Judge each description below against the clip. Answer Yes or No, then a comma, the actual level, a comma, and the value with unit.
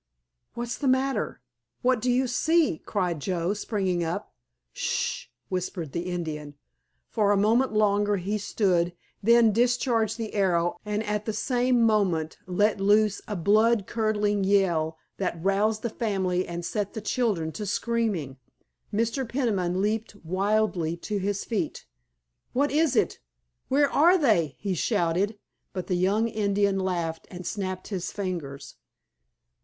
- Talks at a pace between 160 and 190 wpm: No, average, 145 wpm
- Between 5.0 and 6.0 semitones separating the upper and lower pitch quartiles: No, average, 3.8 semitones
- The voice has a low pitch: No, high, 205 Hz